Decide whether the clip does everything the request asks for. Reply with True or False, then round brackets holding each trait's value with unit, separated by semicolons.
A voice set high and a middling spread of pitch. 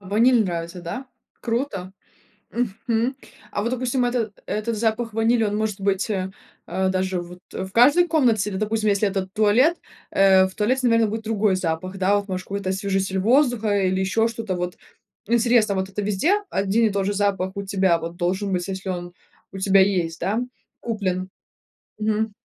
True (200 Hz; 3.1 semitones)